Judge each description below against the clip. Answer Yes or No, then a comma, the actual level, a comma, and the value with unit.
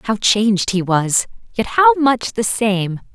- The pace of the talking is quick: No, average, 170 wpm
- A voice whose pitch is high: Yes, high, 220 Hz